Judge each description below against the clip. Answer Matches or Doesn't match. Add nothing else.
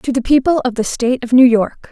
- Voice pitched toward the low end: Doesn't match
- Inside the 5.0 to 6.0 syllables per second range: Matches